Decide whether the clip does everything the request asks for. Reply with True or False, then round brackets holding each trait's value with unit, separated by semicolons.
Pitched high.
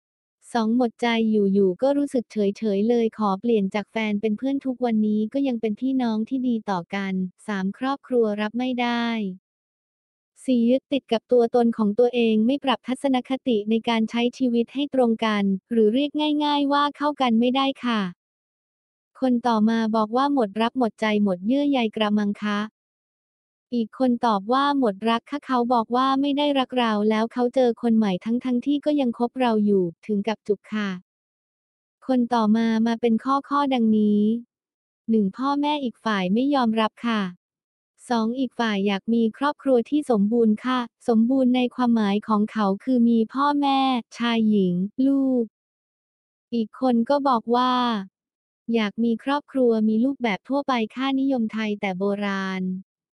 True (235 Hz)